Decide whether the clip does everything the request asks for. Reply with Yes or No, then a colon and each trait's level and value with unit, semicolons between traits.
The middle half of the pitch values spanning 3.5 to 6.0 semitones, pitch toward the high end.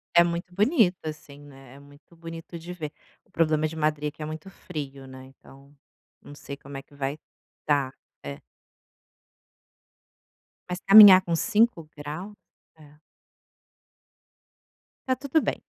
No: average, 3.8 semitones; medium, 155 Hz